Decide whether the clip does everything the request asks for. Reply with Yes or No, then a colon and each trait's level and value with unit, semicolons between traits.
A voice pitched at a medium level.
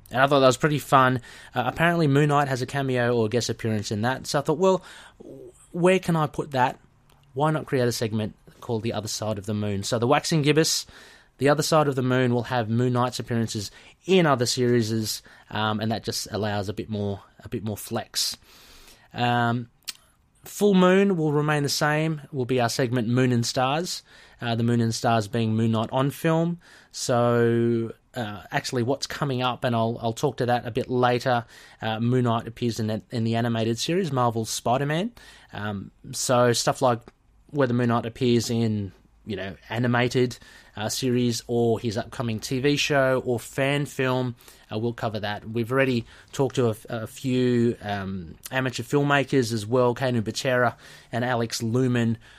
No: low, 125 Hz